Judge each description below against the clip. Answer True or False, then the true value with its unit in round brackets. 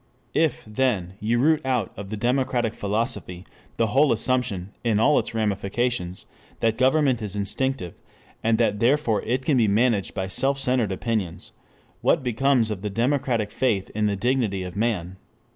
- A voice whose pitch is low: True (115 Hz)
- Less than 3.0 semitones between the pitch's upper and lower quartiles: False (4.0 semitones)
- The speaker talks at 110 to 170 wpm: True (160 wpm)